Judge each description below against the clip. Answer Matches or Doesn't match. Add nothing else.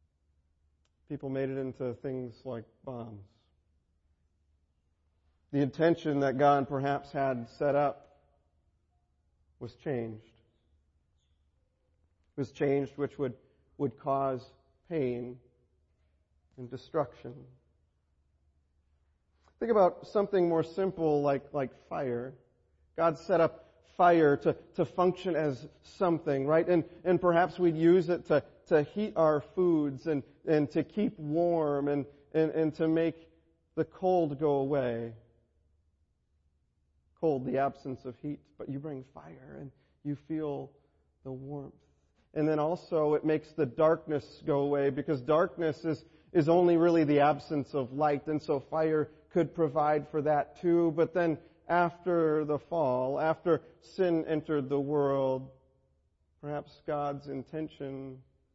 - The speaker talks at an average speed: Doesn't match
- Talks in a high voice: Doesn't match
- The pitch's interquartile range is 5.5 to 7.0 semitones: Matches